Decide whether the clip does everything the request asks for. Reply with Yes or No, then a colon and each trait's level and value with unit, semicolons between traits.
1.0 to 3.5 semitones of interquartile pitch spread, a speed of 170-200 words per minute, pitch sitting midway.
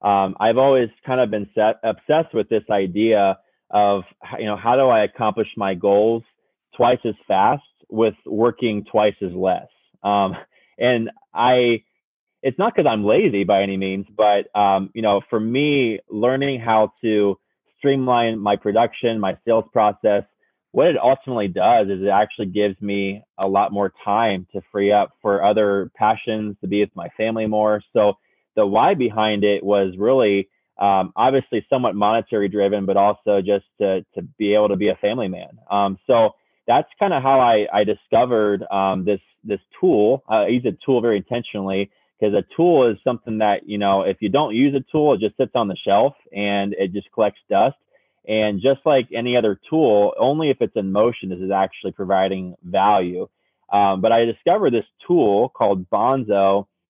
No: average, 2.7 semitones; average, 180 wpm; low, 105 Hz